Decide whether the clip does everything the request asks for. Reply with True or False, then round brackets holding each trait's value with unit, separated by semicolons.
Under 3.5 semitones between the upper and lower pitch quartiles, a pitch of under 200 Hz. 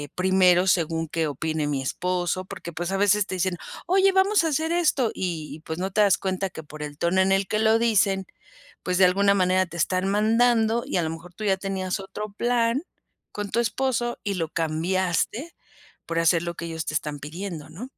False (4.2 semitones; 190 Hz)